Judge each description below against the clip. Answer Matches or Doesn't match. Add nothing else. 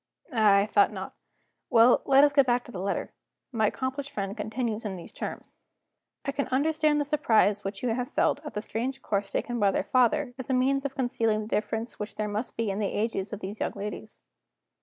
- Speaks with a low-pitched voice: Doesn't match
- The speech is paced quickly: Matches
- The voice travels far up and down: Doesn't match